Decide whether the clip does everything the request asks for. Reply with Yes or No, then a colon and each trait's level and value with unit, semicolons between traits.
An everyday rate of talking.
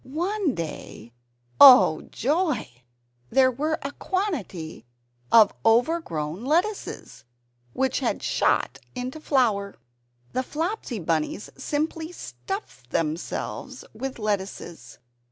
No: slow, 95 wpm